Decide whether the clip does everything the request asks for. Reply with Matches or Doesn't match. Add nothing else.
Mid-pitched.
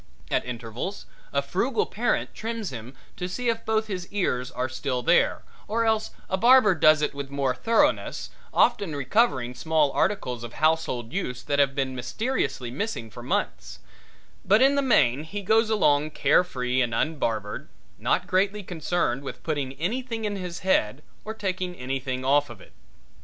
Matches